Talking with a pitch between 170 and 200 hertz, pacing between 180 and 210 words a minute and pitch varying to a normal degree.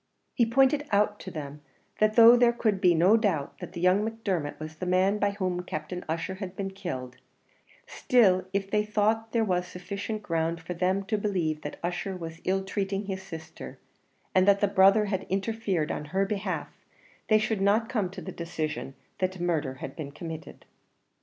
Yes: high, 190 Hz; average, 185 wpm; average, 3.6 semitones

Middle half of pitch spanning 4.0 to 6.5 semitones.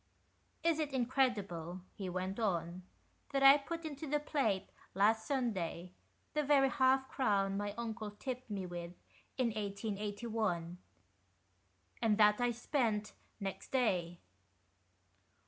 Yes: average, 5.2 semitones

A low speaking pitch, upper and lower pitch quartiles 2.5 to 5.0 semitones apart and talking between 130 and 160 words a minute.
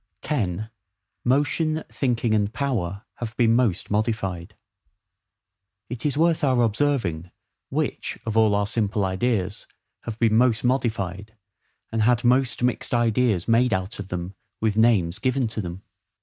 Yes: low, 115 Hz; average, 3.6 semitones; average, 140 wpm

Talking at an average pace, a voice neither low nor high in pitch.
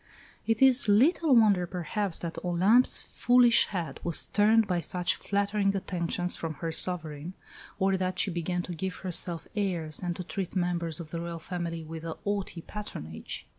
Yes: average, 170 wpm; medium, 180 Hz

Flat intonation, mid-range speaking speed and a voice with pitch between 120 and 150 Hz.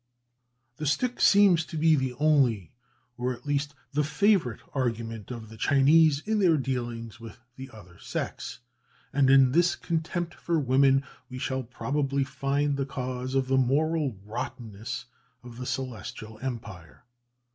No: average, 3.7 semitones; average, 150 wpm; low, 135 Hz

